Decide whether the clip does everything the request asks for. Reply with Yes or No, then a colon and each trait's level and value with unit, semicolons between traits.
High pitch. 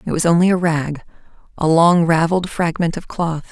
No: medium, 165 Hz